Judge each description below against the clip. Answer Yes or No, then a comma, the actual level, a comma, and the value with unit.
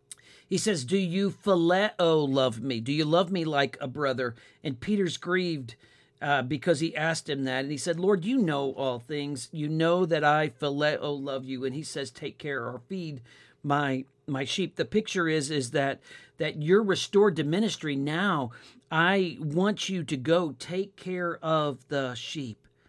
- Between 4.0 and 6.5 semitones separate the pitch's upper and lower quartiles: Yes, average, 4.4 semitones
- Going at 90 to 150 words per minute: No, average, 180 wpm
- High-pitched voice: No, medium, 150 Hz